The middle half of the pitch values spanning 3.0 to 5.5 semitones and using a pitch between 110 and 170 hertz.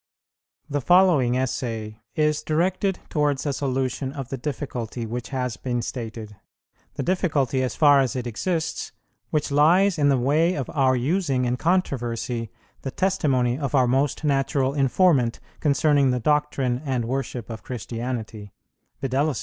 Yes: average, 3.4 semitones; low, 135 Hz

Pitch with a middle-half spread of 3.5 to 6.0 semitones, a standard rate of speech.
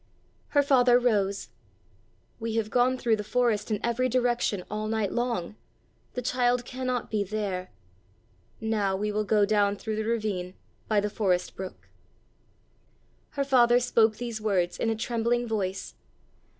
No: average, 2.9 semitones; average, 150 wpm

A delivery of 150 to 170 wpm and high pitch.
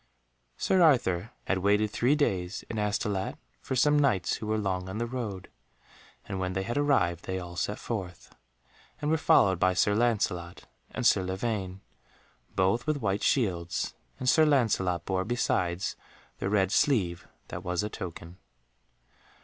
No: average, 155 wpm; low, 100 Hz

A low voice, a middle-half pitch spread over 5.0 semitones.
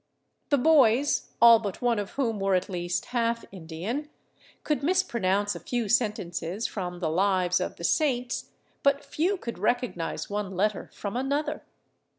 No: high, 225 Hz; wide, 5.6 semitones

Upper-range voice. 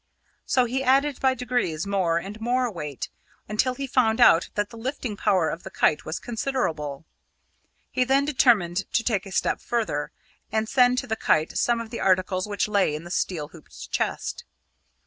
Yes: high, 220 Hz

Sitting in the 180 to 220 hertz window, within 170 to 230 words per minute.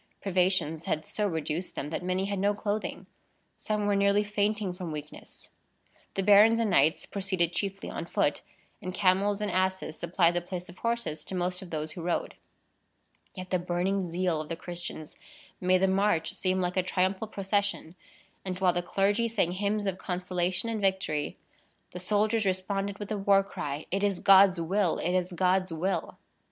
Yes: medium, 185 Hz; average, 180 wpm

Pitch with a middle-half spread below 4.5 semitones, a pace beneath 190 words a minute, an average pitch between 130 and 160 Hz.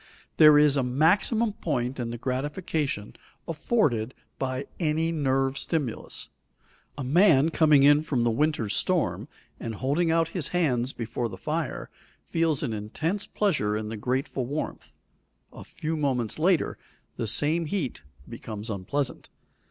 No: average, 5.1 semitones; average, 140 wpm; medium, 140 Hz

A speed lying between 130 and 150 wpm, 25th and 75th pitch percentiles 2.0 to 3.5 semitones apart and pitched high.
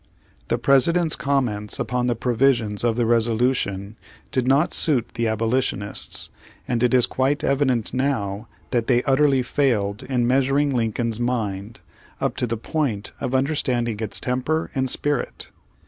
No: average, 145 wpm; average, 3.1 semitones; low, 125 Hz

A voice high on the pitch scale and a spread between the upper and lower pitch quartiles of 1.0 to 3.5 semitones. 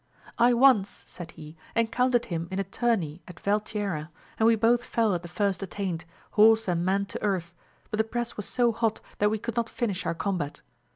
No: high, 205 Hz; average, 4.4 semitones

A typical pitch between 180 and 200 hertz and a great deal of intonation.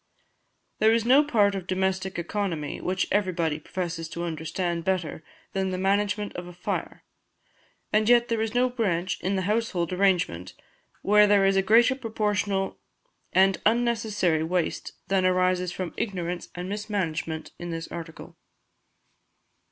No: high, 190 Hz; average, 3.2 semitones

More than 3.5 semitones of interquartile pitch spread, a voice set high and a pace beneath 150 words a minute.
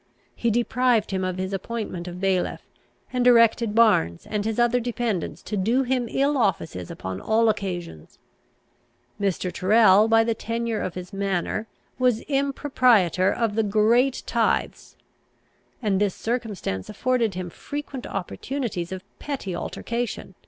Yes: average, 4.2 semitones; high, 220 Hz; average, 140 wpm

